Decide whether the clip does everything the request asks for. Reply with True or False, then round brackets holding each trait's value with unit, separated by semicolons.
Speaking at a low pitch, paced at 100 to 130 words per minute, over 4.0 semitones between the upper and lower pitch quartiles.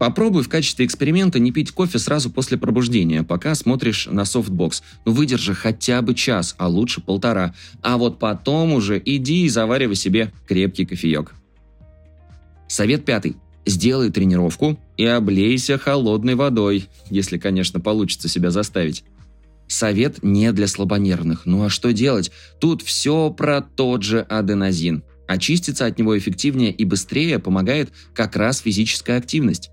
False (105 Hz; 140 wpm; 5.6 semitones)